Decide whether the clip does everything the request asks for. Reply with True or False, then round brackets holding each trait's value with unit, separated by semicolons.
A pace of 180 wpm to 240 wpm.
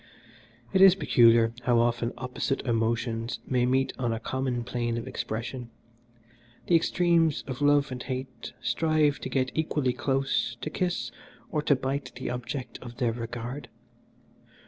False (145 wpm)